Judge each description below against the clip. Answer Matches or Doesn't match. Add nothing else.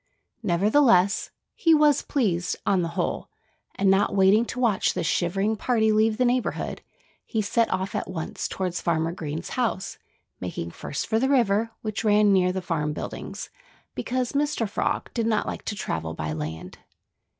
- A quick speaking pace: Doesn't match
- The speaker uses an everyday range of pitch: Matches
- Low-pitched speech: Doesn't match